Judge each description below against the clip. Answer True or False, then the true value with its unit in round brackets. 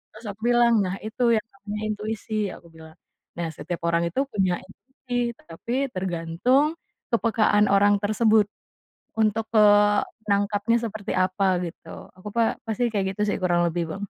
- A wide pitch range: False (3.5 semitones)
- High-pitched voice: True (210 Hz)